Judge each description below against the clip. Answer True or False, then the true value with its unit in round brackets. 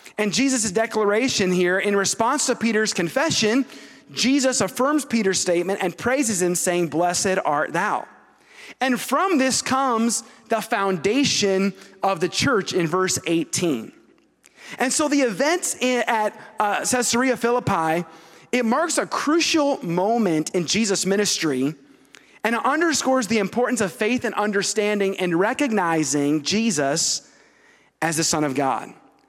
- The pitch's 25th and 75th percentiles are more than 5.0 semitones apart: True (5.4 semitones)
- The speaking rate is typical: False (130 wpm)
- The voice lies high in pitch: True (210 Hz)